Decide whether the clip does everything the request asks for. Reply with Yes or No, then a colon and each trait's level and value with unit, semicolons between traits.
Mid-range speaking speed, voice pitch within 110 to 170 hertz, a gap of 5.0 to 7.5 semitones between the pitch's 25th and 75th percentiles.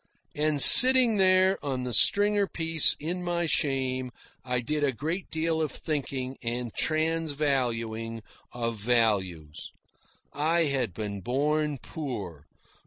No: slow, 120 wpm; medium, 140 Hz; wide, 5.5 semitones